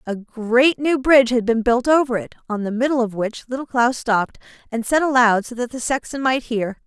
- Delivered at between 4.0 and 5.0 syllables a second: No, 5.3 syllables/s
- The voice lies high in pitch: Yes, high, 240 Hz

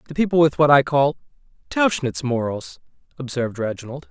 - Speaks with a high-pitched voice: No, medium, 140 Hz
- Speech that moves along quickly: No, average, 145 wpm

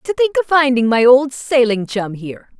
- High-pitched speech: Yes, very high, 260 Hz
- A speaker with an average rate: No, fast, 210 wpm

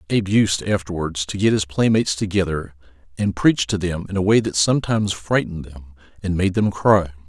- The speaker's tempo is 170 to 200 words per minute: Yes, average, 190 wpm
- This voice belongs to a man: Yes, male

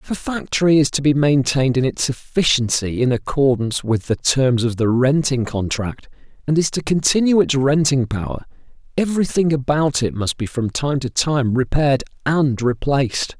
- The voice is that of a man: Yes, male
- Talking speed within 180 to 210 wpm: No, average, 170 wpm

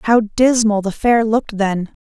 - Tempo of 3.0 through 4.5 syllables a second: Yes, 4.4 syllables/s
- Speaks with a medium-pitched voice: No, high, 220 Hz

